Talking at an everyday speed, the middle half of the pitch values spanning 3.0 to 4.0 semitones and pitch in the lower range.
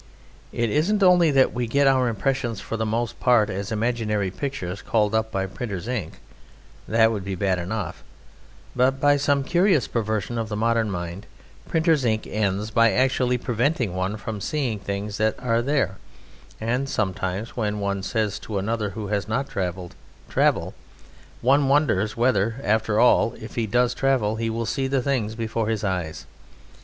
Yes: average, 170 wpm; average, 3.6 semitones; low, 110 Hz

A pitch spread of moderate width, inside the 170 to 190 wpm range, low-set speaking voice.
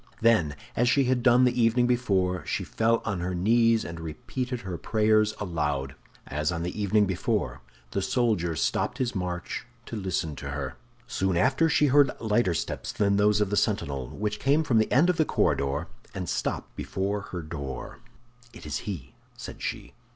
No: wide, 6.1 semitones; average, 180 wpm; low, 100 Hz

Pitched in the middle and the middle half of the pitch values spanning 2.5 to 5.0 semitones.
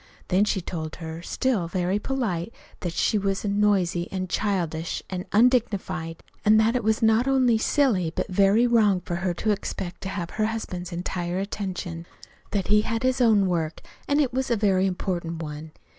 No: high, 195 Hz; average, 4.0 semitones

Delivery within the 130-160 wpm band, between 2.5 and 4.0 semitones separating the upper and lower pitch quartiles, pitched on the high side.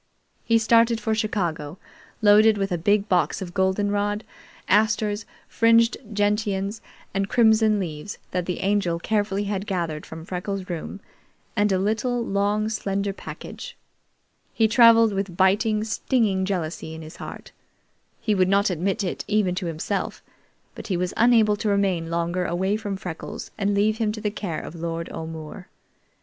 Yes: average, 155 wpm; average, 3.0 semitones; high, 200 Hz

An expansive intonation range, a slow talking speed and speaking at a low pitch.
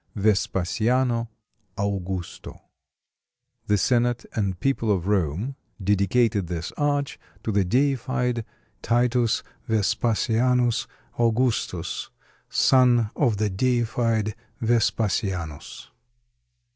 No: average, 3.6 semitones; slow, 80 wpm; low, 115 Hz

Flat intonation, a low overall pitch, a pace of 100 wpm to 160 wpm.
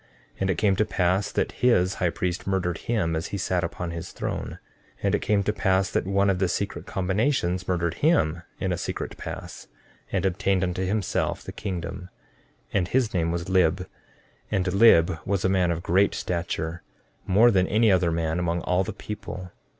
No: narrow, 2.2 semitones; very low, 95 Hz; average, 195 wpm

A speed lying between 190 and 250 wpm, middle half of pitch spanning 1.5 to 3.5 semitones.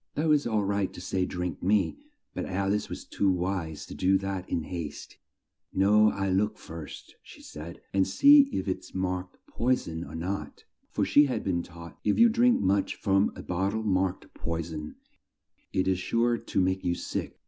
Yes: average, 195 wpm; average, 2.8 semitones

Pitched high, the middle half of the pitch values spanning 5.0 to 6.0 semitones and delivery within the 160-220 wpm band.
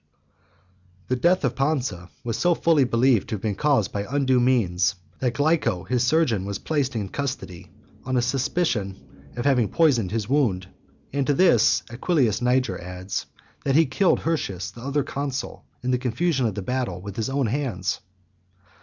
No: low, 125 Hz; wide, 5.4 semitones; average, 170 wpm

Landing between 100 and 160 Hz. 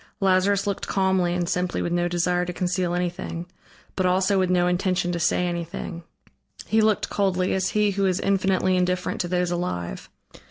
No: medium, 180 Hz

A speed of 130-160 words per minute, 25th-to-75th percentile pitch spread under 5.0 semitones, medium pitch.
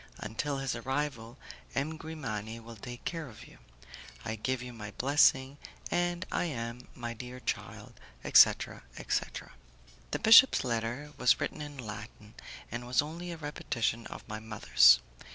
No: average, 150 wpm; average, 4.5 semitones; low, 125 Hz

